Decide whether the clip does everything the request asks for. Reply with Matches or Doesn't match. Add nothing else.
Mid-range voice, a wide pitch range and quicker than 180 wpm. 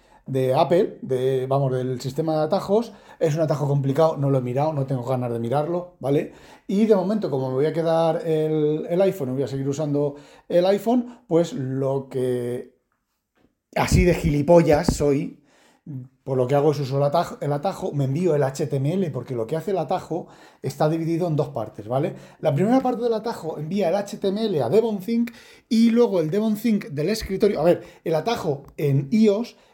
Matches